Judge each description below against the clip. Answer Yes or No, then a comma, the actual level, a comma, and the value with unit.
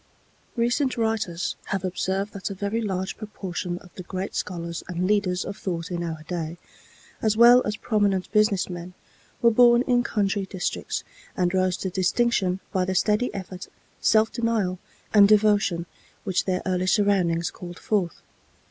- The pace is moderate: Yes, average, 155 wpm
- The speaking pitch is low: No, high, 190 Hz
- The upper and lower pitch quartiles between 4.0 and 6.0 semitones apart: No, average, 2.8 semitones